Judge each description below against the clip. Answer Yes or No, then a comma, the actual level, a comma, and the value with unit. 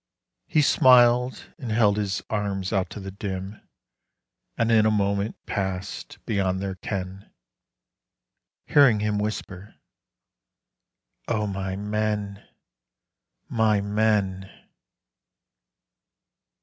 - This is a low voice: Yes, low, 105 Hz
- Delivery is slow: Yes, slow, 95 wpm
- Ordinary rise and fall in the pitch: No, narrow, 2.0 semitones